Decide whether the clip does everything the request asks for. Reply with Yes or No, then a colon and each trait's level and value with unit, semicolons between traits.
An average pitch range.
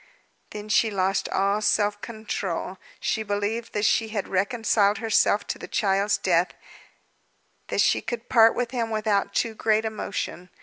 No: narrow, 1.9 semitones